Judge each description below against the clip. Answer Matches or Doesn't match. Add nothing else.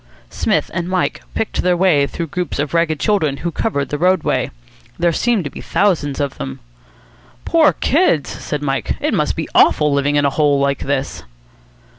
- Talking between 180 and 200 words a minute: Matches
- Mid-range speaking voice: Matches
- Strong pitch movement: Doesn't match